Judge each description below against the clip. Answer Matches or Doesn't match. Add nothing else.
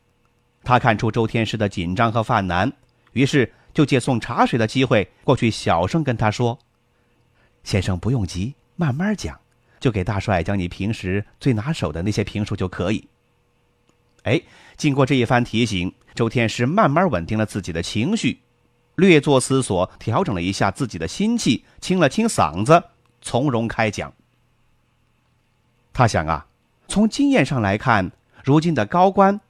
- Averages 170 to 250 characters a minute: Matches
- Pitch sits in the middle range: Doesn't match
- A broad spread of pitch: Doesn't match